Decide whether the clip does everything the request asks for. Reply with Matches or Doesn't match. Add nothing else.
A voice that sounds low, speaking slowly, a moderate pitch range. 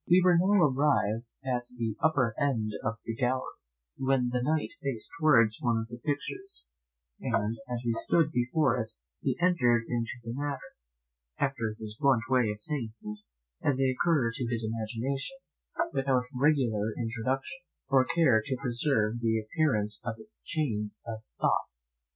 Doesn't match